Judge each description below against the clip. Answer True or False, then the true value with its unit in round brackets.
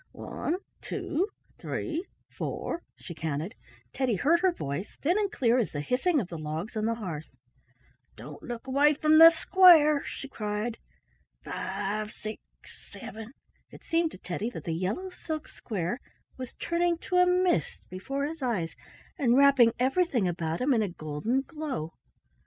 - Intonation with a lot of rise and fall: True (9.0 semitones)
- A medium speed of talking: True (145 wpm)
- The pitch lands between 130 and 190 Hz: False (245 Hz)